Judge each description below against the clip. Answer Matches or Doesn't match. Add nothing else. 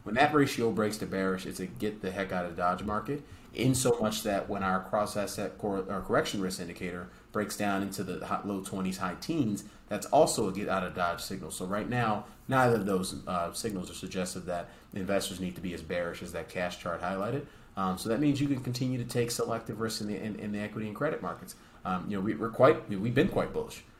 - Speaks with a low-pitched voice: Matches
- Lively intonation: Doesn't match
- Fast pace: Matches